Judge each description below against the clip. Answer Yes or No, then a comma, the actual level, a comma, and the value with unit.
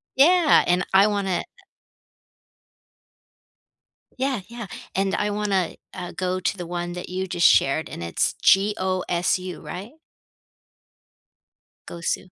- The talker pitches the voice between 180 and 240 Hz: Yes, medium, 185 Hz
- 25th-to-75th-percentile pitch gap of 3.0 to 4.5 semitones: No, narrow, 2.6 semitones